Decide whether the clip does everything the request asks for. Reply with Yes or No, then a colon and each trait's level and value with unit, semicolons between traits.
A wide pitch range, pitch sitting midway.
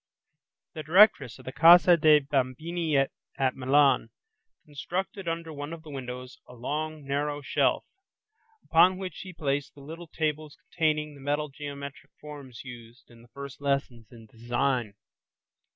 No: average, 3.1 semitones; medium, 145 Hz